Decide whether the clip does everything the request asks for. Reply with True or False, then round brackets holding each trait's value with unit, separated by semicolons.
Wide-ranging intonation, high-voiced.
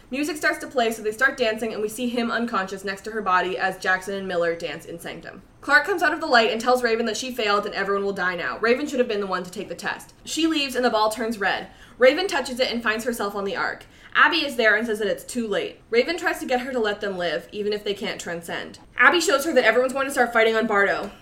False (4.3 semitones; 225 Hz)